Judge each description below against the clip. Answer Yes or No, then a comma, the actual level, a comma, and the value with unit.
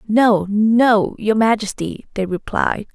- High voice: Yes, high, 215 Hz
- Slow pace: Yes, slow, 120 wpm